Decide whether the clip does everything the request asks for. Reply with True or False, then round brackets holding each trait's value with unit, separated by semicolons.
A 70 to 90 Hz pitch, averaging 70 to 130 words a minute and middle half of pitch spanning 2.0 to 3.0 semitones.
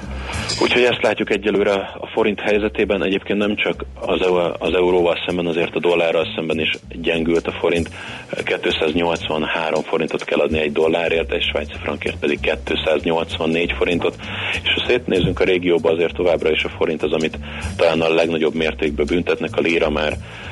False (85 Hz; 155 wpm; 2.6 semitones)